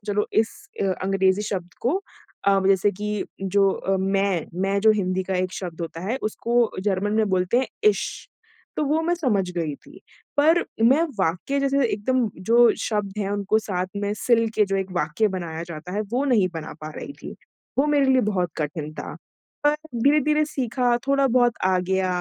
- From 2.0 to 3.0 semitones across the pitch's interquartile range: No, average, 4.5 semitones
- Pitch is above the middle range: Yes, high, 205 Hz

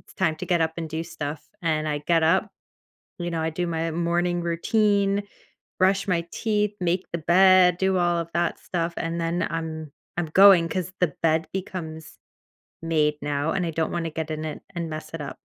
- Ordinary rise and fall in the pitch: No, narrow, 2.0 semitones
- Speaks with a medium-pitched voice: Yes, medium, 170 Hz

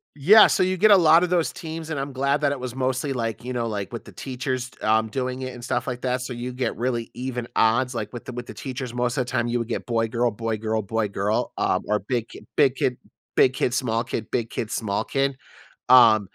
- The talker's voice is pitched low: Yes, low, 125 Hz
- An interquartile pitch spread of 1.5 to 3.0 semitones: Yes, narrow, 2.6 semitones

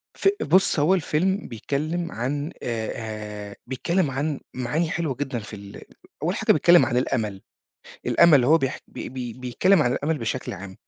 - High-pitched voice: No, low, 135 Hz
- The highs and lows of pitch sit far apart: Yes, wide, 5.9 semitones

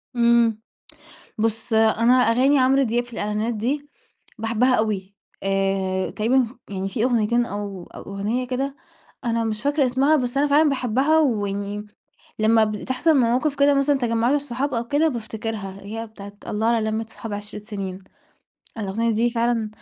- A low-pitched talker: No, high, 230 Hz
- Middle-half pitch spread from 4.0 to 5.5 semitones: No, average, 3.4 semitones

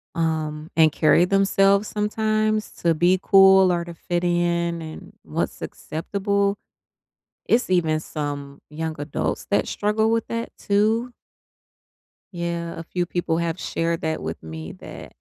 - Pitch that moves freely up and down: No, average, 3.9 semitones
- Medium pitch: Yes, medium, 175 Hz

